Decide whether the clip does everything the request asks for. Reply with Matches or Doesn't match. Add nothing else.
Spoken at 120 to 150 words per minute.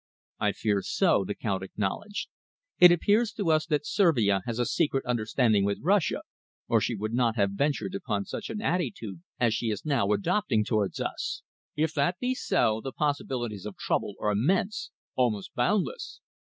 Doesn't match